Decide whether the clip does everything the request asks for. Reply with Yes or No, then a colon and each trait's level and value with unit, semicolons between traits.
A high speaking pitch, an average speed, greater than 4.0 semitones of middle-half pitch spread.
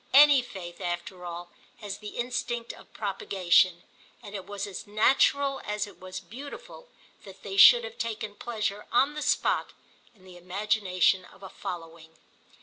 Yes: high, 205 Hz; average, 155 wpm; average, 4.7 semitones